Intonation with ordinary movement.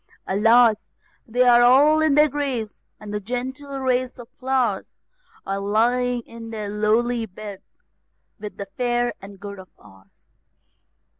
Yes: average, 3.3 semitones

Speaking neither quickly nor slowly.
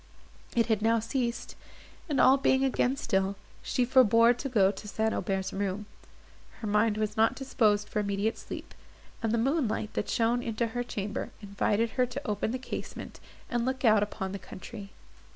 Yes: average, 175 wpm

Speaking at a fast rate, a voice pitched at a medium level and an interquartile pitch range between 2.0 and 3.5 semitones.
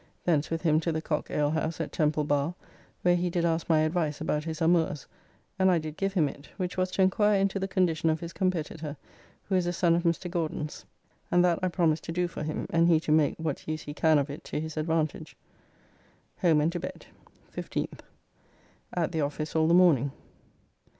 Yes: fast, 210 wpm; medium, 165 Hz; narrow, 2.4 semitones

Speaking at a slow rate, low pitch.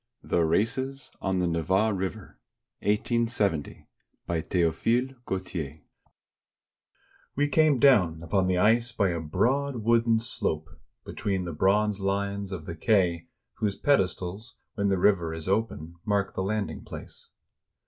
Yes: slow, 130 wpm; low, 100 Hz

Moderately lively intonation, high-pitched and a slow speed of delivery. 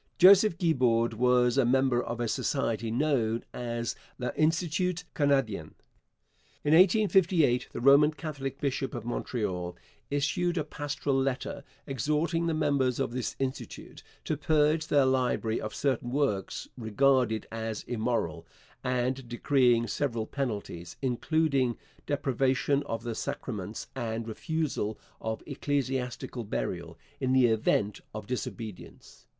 No: average, 3.9 semitones; low, 130 Hz; slow, 120 wpm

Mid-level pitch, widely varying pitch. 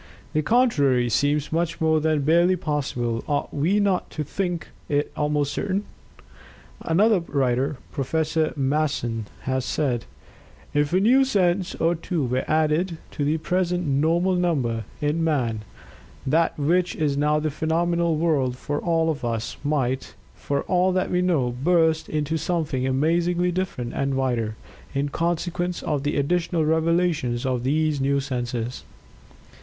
No: medium, 155 Hz; average, 4.0 semitones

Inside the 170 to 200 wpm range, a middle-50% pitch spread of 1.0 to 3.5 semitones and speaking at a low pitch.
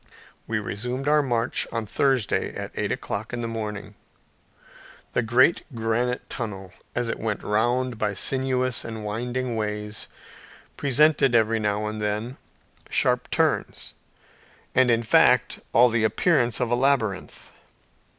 No: slow, 135 wpm; average, 2.9 semitones; low, 115 Hz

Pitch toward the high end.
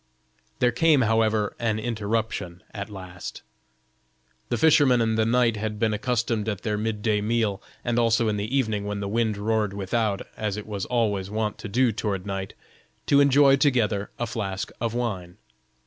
No: low, 110 Hz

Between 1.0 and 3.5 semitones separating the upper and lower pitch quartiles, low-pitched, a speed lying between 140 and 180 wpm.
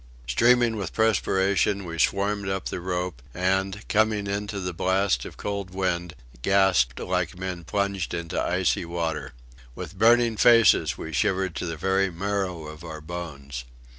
Yes: average, 3.0 semitones; very low, 95 Hz; average, 150 wpm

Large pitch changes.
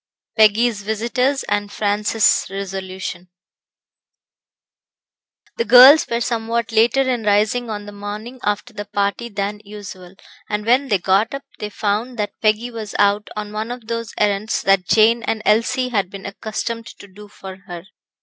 No: narrow, 2.4 semitones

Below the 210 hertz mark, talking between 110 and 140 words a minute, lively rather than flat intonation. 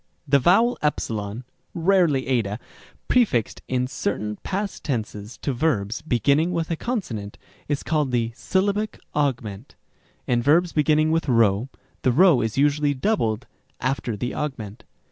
Yes: low, 135 Hz; slow, 135 wpm; wide, 5.9 semitones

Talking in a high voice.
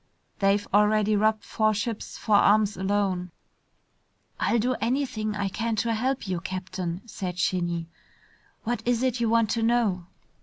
Yes: high, 210 Hz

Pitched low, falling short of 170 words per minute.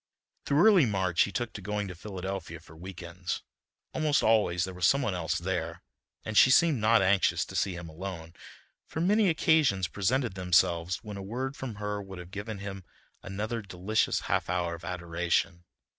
No: very low, 95 Hz; average, 185 wpm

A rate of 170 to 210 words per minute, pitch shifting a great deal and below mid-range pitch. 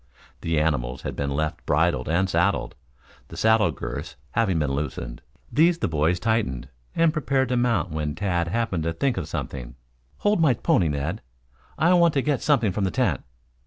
Yes: average, 180 wpm; wide, 8.5 semitones; very low, 90 Hz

